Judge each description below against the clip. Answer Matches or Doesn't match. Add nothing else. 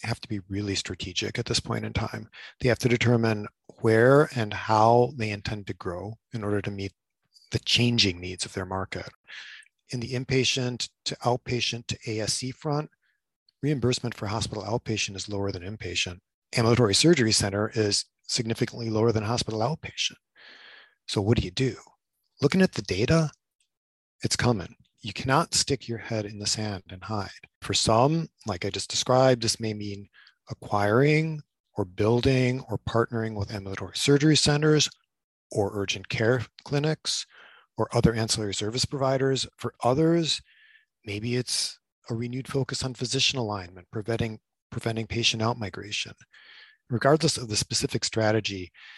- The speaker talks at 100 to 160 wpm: Matches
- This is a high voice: Doesn't match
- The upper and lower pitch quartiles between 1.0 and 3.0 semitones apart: Doesn't match